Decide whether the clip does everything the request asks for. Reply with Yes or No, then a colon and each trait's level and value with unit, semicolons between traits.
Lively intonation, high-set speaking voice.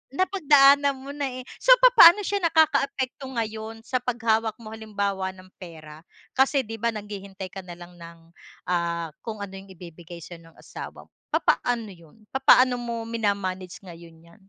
Yes: wide, 6.3 semitones; high, 215 Hz